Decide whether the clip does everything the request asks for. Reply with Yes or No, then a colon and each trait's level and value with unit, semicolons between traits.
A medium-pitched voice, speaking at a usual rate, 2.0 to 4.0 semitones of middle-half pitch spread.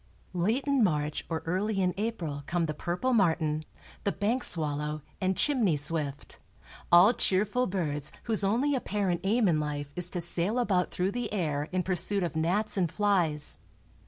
No: medium, 180 Hz; average, 165 wpm; average, 4.8 semitones